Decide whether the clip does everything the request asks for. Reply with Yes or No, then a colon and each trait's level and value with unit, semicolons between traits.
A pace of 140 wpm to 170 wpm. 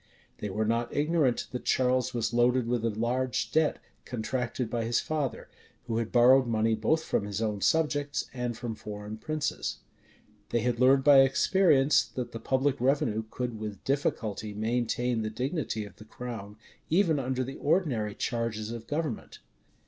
Yes: average, 165 wpm